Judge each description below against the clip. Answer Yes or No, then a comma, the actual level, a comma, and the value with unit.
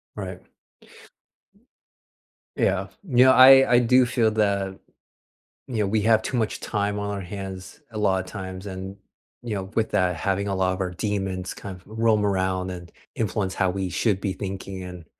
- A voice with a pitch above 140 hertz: No, low, 100 Hz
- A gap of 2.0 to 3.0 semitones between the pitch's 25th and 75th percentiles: Yes, average, 2.7 semitones